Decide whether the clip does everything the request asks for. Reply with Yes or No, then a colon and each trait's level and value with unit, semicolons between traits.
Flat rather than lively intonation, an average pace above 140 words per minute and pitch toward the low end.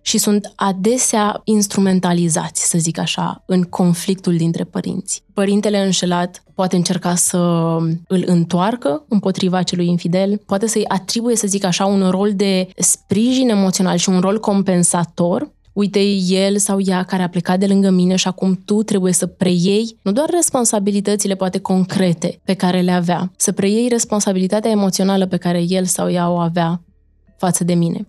No: narrow, 2.3 semitones; average, 160 wpm; high, 190 Hz